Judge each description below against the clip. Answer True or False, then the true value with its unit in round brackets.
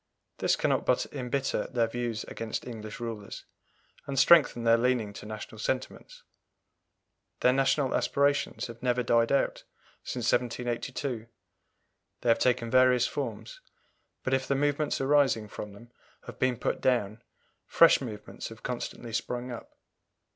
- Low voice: True (125 Hz)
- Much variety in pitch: False (2.5 semitones)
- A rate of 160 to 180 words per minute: False (140 wpm)